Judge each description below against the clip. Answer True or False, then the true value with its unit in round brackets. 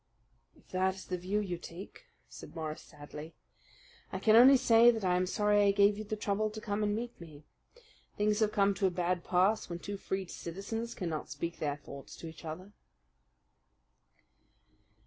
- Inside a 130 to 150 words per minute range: False (185 wpm)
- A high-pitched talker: True (195 Hz)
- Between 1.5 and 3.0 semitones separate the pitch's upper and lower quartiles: False (3.5 semitones)